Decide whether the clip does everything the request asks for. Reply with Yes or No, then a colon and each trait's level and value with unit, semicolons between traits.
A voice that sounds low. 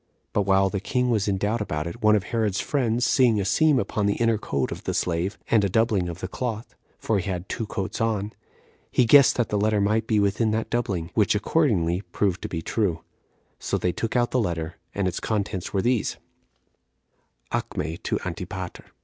Yes: low, 105 Hz